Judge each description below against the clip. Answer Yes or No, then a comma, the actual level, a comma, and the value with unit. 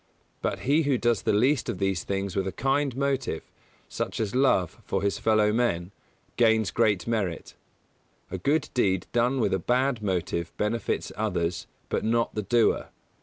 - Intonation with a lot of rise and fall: No, average, 4.3 semitones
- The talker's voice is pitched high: No, low, 110 Hz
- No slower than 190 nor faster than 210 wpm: No, average, 170 wpm